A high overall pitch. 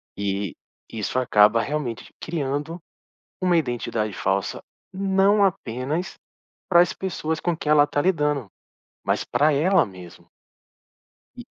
No: medium, 150 Hz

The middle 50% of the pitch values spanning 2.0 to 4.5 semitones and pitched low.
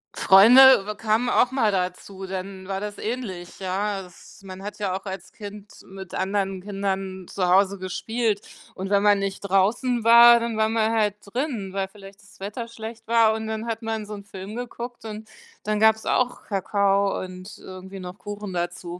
No: narrow, 2.5 semitones; high, 200 Hz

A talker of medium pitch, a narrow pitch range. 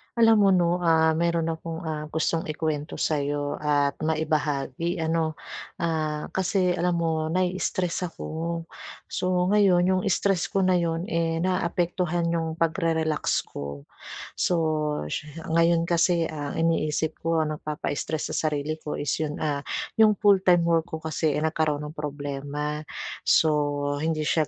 Yes: medium, 160 Hz; narrow, 2.2 semitones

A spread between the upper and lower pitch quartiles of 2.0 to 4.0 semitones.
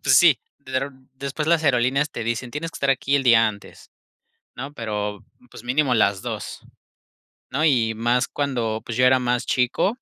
Yes: average, 3.2 semitones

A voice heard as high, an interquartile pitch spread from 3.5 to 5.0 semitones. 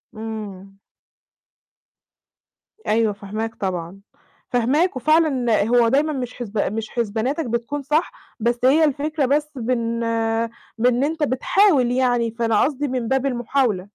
Yes: high, 245 Hz; average, 4.0 semitones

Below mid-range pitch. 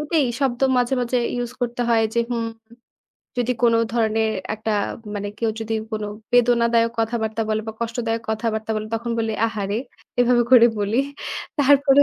No: high, 230 Hz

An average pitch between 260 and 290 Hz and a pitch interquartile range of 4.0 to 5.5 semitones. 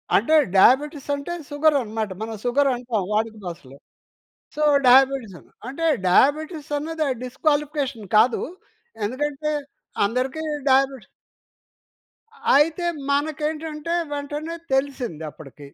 Yes: very high, 275 Hz; average, 4.4 semitones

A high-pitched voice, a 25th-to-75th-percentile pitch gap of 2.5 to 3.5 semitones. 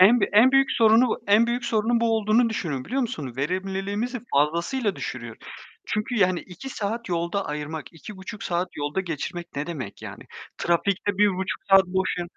No: high, 195 Hz; average, 4.8 semitones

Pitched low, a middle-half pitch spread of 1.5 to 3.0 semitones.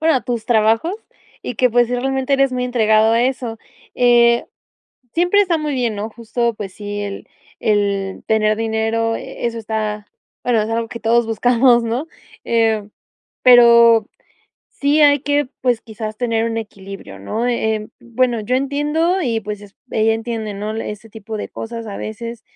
No: high, 230 Hz; narrow, 2.4 semitones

